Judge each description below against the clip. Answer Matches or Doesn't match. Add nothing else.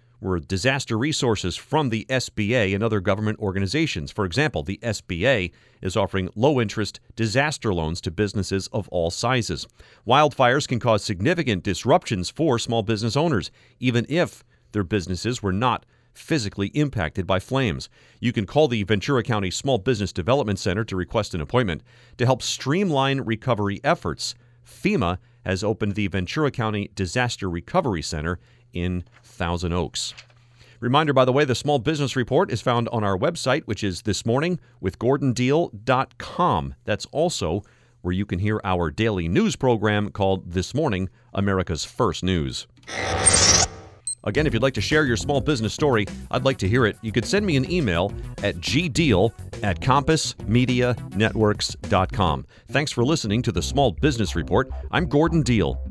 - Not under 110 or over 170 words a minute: Matches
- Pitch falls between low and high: Doesn't match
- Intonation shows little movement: Doesn't match